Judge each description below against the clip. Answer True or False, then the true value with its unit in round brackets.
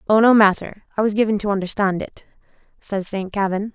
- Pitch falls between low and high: False (205 Hz)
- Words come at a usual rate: True (190 wpm)